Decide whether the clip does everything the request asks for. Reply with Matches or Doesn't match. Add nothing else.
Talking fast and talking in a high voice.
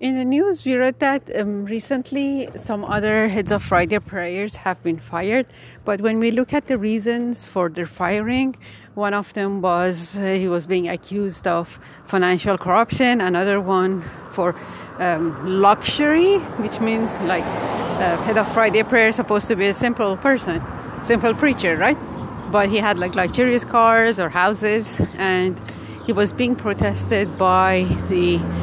Matches